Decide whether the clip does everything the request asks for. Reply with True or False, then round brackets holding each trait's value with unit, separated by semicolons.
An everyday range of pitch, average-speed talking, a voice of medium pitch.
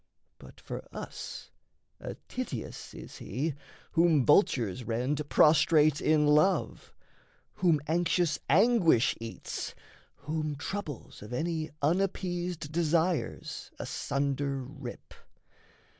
False (3.7 semitones; 95 wpm; 155 Hz)